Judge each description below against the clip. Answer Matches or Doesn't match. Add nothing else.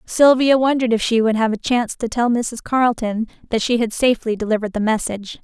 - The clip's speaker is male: Doesn't match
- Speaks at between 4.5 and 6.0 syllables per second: Doesn't match